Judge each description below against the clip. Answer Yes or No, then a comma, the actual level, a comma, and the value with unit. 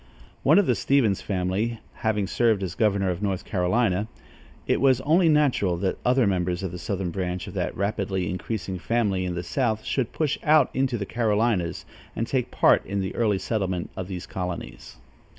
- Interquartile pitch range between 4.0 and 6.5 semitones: Yes, average, 4.4 semitones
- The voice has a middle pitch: No, low, 100 Hz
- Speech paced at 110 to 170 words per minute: No, average, 185 wpm